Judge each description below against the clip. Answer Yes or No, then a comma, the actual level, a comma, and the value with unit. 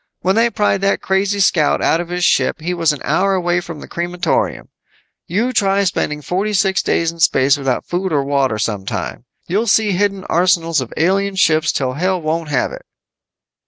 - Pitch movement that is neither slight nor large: Yes, average, 3.9 semitones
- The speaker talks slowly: No, average, 190 wpm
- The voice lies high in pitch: No, medium, 175 Hz